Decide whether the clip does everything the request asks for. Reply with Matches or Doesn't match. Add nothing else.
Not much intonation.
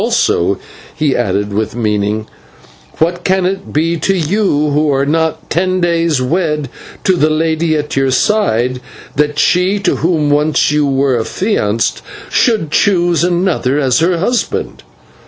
Doesn't match